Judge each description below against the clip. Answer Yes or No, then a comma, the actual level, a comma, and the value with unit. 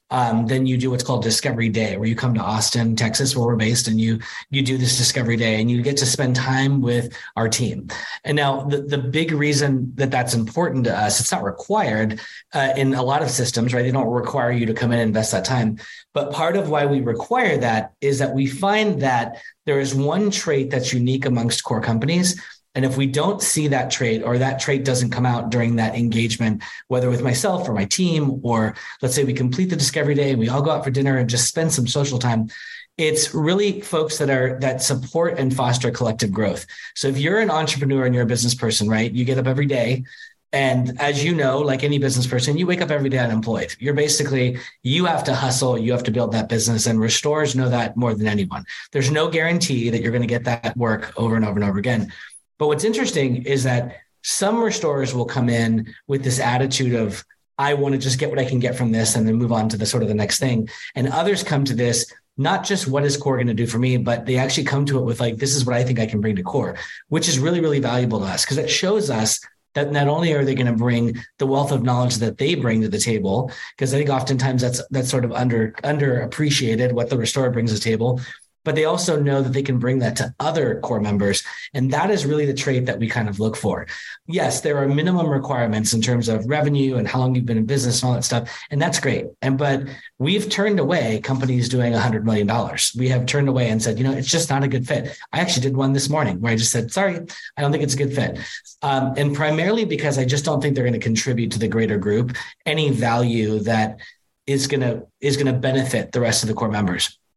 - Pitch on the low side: Yes, low, 130 Hz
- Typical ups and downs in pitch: Yes, average, 3.3 semitones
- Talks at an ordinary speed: No, fast, 250 wpm